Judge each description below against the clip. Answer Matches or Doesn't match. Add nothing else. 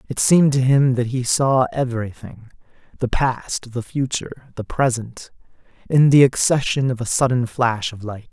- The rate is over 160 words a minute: Doesn't match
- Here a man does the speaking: Matches